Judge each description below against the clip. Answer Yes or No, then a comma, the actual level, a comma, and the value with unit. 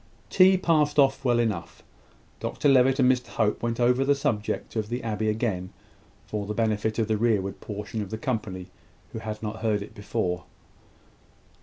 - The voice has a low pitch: Yes, low, 110 Hz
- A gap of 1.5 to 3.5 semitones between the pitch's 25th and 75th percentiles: Yes, average, 3.1 semitones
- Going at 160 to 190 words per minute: Yes, average, 175 wpm